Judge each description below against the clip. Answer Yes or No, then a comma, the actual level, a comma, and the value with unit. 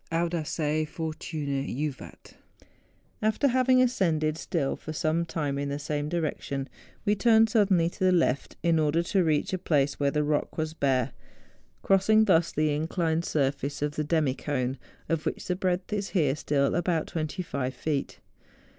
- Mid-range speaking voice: Yes, medium, 155 Hz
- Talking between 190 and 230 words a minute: No, average, 160 wpm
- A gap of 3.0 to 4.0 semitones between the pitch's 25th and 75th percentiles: Yes, average, 3.4 semitones